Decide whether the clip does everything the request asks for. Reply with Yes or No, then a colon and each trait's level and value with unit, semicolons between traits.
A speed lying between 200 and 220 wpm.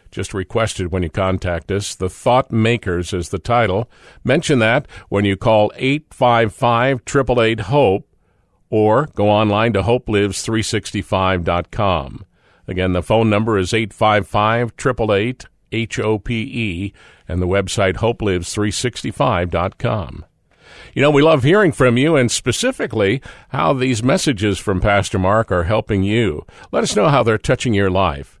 No: slow, 135 wpm